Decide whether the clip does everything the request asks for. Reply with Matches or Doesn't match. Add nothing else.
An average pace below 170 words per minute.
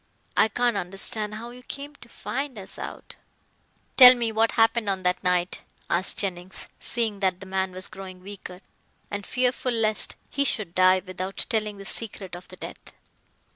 Doesn't match